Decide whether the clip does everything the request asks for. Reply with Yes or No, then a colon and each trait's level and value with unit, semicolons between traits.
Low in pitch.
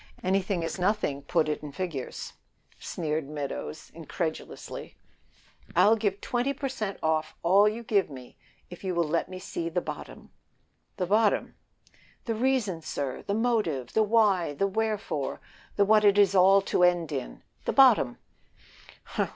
No: medium, 185 Hz